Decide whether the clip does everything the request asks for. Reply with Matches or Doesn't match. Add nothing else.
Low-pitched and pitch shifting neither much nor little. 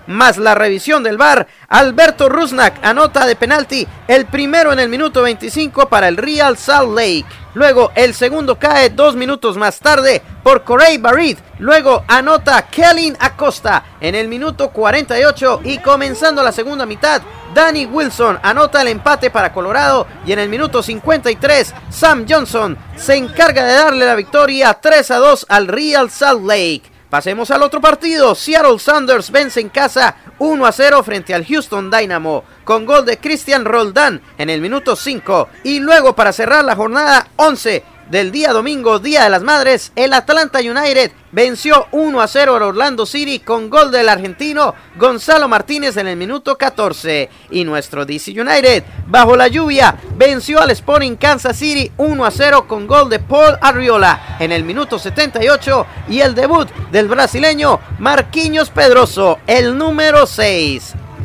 Doesn't match